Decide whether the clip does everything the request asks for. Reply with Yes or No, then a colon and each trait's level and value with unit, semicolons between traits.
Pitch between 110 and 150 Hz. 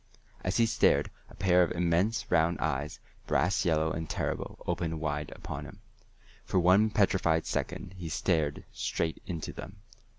No: very low, 85 Hz